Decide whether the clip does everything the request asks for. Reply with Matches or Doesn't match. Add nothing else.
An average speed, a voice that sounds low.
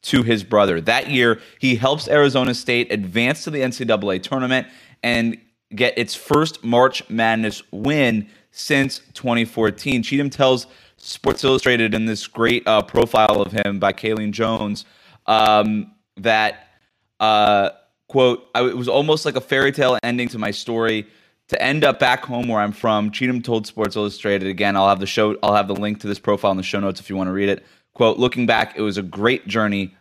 Matches